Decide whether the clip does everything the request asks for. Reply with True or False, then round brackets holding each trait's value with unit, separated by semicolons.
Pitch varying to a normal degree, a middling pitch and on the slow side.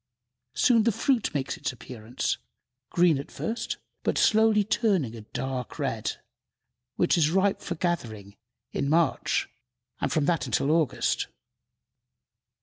False (7.6 semitones; 160 Hz; 130 wpm)